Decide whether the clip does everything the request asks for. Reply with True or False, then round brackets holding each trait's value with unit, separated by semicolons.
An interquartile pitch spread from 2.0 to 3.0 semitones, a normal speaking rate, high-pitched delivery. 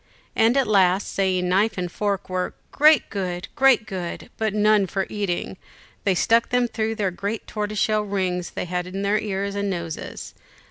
True (2.7 semitones; 180 wpm; 200 Hz)